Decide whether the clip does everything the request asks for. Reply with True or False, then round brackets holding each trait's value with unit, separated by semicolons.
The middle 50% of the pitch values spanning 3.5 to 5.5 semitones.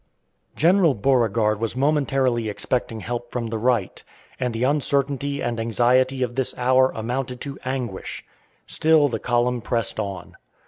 False (2.7 semitones)